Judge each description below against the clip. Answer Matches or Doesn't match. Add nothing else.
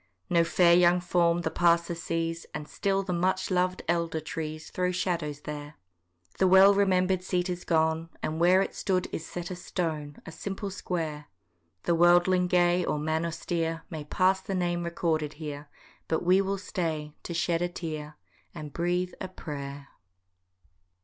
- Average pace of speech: Matches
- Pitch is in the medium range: Matches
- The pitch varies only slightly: Matches